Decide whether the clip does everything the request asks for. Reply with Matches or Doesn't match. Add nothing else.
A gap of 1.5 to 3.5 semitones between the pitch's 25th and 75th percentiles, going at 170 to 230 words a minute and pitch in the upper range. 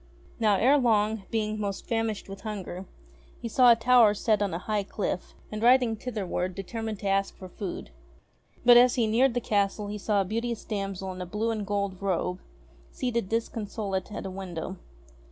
Matches